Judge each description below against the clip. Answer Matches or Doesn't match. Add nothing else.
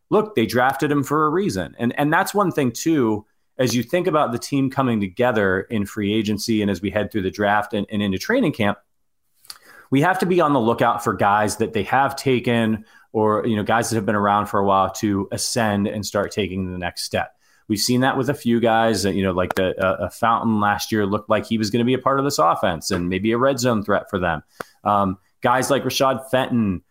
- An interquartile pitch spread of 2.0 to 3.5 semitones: Doesn't match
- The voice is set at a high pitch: Doesn't match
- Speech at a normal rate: Doesn't match